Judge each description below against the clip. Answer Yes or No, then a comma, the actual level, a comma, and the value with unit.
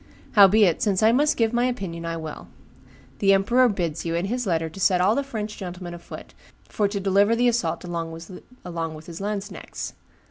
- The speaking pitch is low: No, high, 195 Hz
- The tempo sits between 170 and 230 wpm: Yes, average, 180 wpm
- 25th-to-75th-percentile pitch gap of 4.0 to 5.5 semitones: Yes, average, 4.5 semitones